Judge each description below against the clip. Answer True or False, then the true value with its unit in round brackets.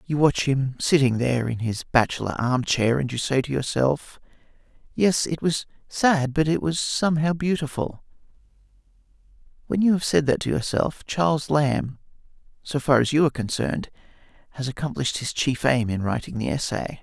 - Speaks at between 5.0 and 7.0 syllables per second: True (5.2 syllables/s)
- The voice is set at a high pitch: False (140 Hz)